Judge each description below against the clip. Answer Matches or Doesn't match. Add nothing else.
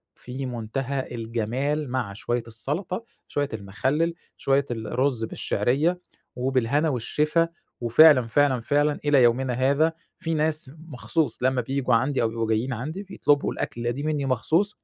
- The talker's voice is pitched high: Doesn't match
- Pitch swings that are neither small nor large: Matches